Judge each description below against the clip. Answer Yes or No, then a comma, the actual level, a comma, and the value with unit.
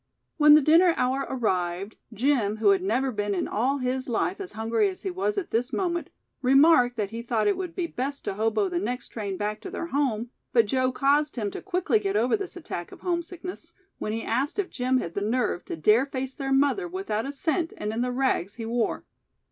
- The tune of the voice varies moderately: No, wide, 6.2 semitones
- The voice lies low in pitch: No, very high, 255 Hz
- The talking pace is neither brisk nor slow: No, fast, 225 wpm